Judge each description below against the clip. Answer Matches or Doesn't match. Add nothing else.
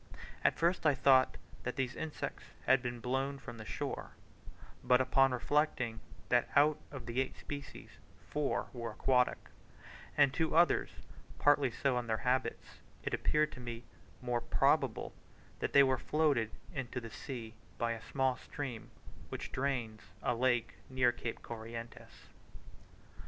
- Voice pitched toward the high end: Doesn't match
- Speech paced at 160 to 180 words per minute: Doesn't match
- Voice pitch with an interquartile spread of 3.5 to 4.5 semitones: Doesn't match